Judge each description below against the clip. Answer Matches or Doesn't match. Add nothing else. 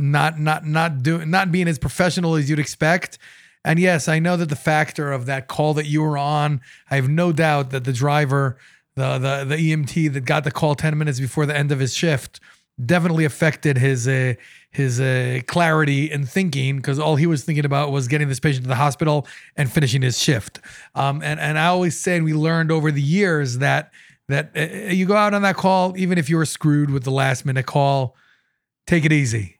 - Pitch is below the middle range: Doesn't match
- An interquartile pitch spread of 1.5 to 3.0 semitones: Matches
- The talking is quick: Matches